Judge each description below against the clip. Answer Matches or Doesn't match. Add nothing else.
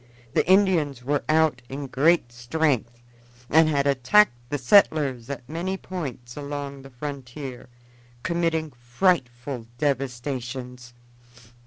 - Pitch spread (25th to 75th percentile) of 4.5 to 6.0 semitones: Doesn't match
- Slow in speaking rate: Matches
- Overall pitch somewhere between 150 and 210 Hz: Doesn't match